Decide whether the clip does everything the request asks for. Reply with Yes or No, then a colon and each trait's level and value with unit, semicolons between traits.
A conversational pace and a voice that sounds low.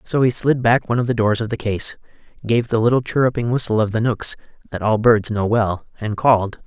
No: fast, 235 wpm; low, 115 Hz